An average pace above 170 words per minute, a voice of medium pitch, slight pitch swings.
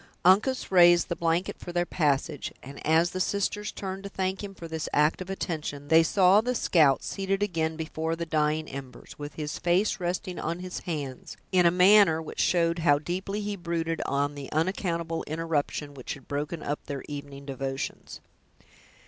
No: average, 180 wpm; medium, 165 Hz; average, 3.8 semitones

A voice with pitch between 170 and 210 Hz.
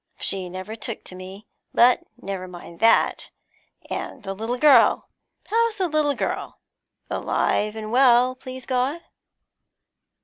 No: high, 235 Hz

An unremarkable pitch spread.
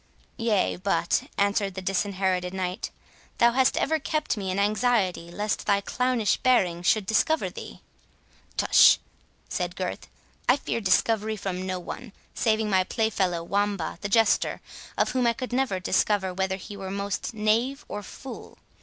Yes: average, 3.5 semitones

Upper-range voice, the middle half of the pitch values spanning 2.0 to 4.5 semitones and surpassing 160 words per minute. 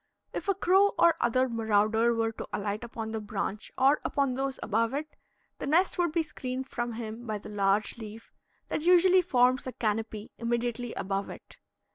Yes: high, 235 Hz; average, 4.0 semitones; average, 180 wpm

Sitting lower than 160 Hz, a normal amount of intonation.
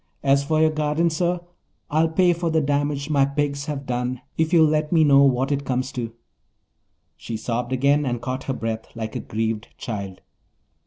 Yes: medium, 140 Hz; average, 3.8 semitones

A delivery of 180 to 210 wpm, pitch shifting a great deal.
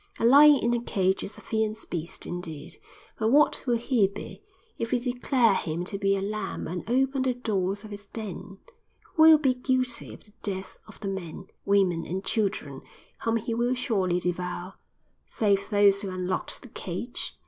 No: average, 185 wpm; average, 4.2 semitones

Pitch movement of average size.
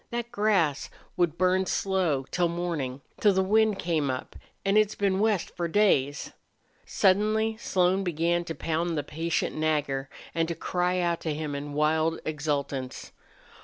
Yes: average, 4.1 semitones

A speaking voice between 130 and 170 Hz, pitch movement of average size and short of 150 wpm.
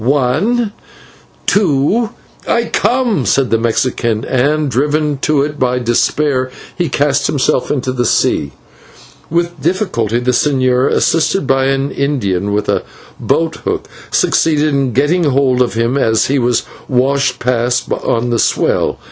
Yes: low, 135 Hz; average, 3.6 semitones; average, 140 wpm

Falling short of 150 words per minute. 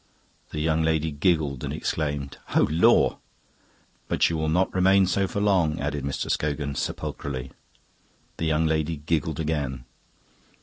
Yes: average, 140 wpm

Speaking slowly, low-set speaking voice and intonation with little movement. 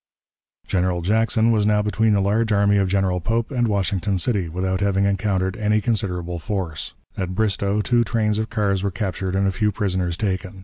No: average, 185 wpm; low, 100 Hz; narrow, 2.3 semitones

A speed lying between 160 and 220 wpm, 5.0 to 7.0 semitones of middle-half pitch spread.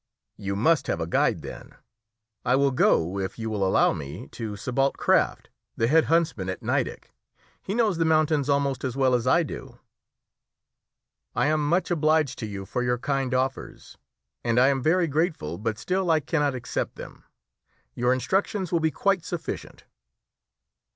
Yes: average, 170 wpm; wide, 5.5 semitones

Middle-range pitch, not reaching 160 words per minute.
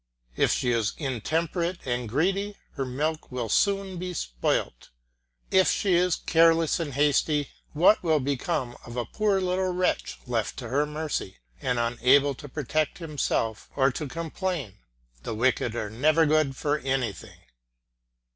Yes: medium, 145 Hz; average, 150 wpm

